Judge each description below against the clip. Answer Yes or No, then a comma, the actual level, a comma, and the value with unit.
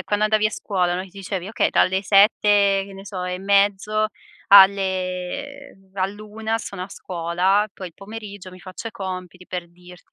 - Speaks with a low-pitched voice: No, high, 195 Hz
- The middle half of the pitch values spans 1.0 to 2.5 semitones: Yes, narrow, 2.1 semitones